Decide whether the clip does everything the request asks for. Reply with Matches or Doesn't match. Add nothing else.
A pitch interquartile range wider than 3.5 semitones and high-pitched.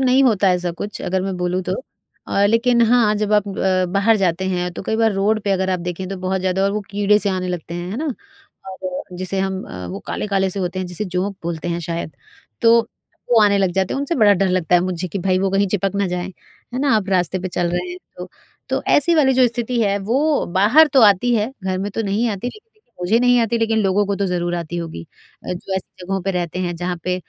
Doesn't match